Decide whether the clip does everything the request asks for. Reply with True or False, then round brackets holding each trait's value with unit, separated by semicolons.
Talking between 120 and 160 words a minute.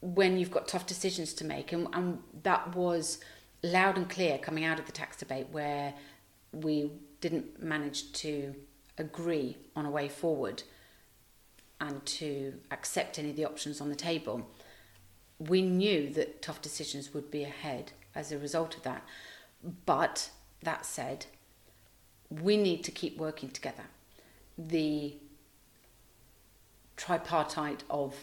True (140 wpm)